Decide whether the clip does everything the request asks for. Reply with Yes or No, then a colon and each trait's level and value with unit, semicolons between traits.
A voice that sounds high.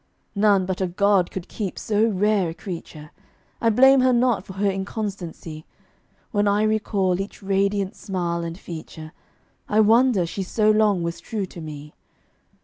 Yes: high, 195 Hz